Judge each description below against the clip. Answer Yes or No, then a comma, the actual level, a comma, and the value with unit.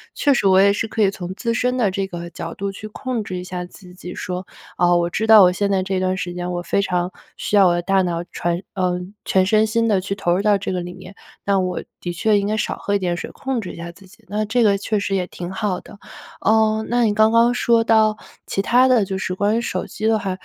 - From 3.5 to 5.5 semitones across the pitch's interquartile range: No, average, 3.1 semitones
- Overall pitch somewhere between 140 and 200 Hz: Yes, high, 195 Hz